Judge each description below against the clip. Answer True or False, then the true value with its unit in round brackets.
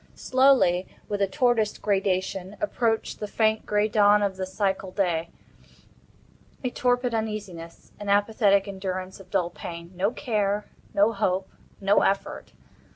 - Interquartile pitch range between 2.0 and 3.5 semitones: True (2.4 semitones)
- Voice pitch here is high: True (200 Hz)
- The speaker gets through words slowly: True (115 wpm)